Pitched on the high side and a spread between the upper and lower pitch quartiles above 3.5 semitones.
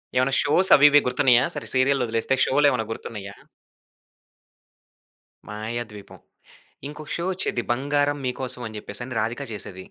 No: low, 125 Hz; average, 4.3 semitones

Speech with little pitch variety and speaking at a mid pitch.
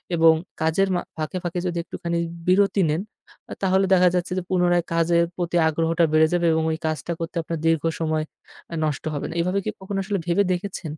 Yes: narrow, 2.1 semitones; medium, 170 Hz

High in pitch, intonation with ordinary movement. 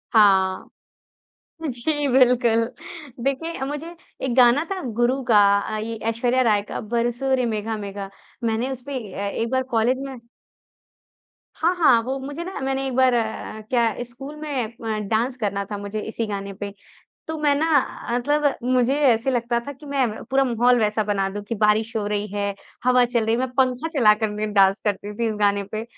Yes: high, 235 Hz; average, 3.7 semitones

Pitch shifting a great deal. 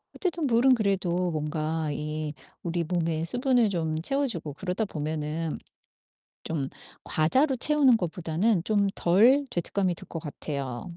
Yes: wide, 6.3 semitones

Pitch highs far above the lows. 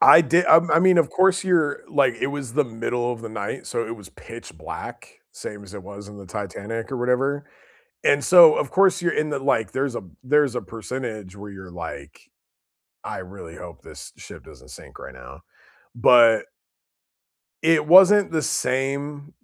Yes: wide, 6.5 semitones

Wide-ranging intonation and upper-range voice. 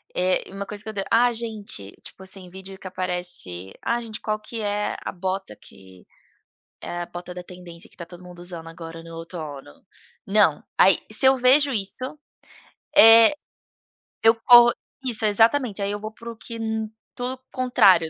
No: average, 4.3 semitones; high, 195 Hz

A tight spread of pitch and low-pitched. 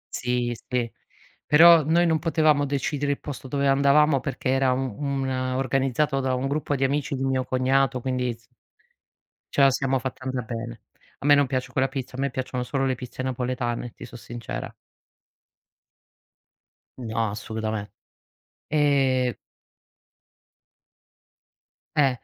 Yes: narrow, 1.9 semitones; low, 130 Hz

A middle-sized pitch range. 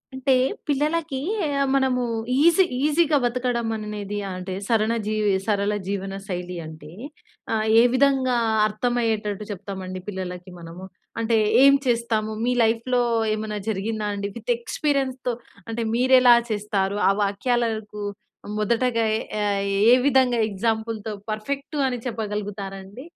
Yes: average, 3.6 semitones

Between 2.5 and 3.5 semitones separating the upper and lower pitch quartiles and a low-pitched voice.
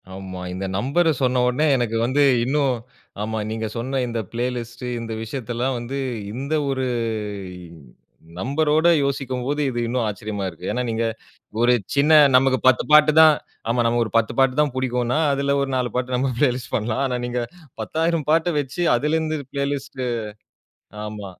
Yes: average, 3.1 semitones; low, 130 Hz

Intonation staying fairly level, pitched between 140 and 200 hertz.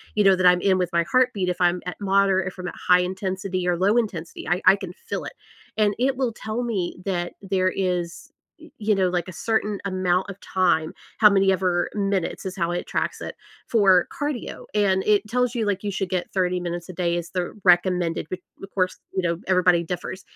Yes: narrow, 2.1 semitones; medium, 185 Hz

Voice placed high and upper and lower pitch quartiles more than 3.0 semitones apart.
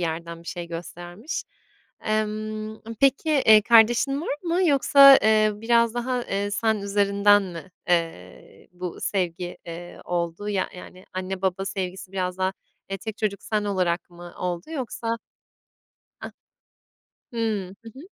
Yes: high, 200 Hz; average, 4.0 semitones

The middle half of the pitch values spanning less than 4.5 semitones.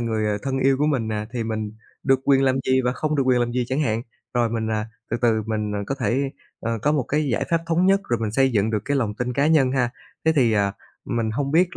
Yes: average, 3.8 semitones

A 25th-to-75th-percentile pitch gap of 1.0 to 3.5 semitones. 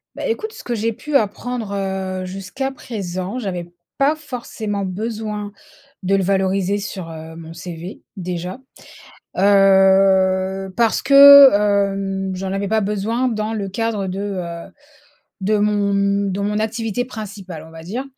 Yes: average, 2.7 semitones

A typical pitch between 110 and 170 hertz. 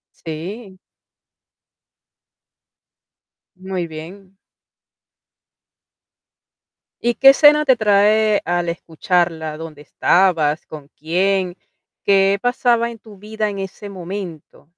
No: high, 195 Hz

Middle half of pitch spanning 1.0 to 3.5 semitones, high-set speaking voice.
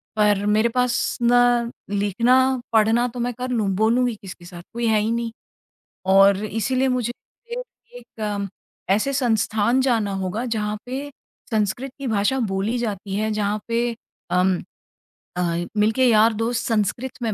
Yes: average, 2.8 semitones; high, 225 Hz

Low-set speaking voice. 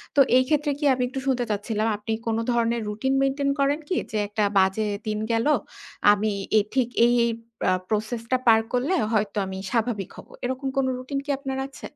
No: high, 235 Hz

